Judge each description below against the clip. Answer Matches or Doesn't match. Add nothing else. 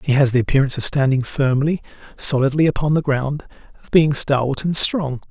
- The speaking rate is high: Doesn't match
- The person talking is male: Matches